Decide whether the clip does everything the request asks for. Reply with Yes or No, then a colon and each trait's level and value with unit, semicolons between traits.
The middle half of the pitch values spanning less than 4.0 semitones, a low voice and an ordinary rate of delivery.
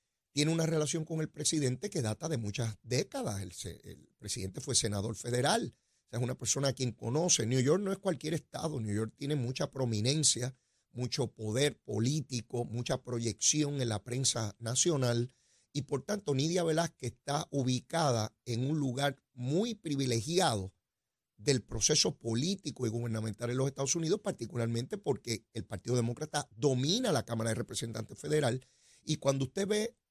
No: average, 4.5 semitones; low, 130 Hz; average, 160 wpm